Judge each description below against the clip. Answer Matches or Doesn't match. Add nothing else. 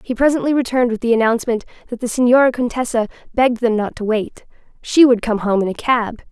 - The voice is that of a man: Doesn't match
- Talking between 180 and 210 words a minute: Matches